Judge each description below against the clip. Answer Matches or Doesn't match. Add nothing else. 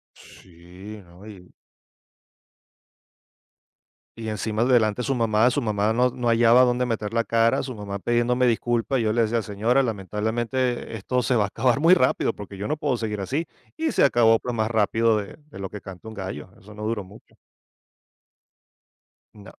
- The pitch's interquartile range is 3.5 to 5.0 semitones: Doesn't match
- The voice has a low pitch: Matches